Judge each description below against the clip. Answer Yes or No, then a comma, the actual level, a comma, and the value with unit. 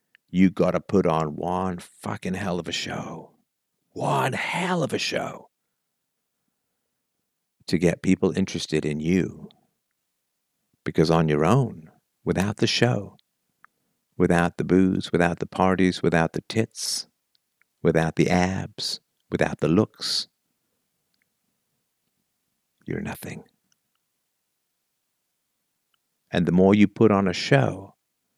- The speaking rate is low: Yes, slow, 110 wpm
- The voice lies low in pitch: Yes, very low, 90 Hz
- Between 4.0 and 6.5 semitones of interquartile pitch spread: No, narrow, 2.5 semitones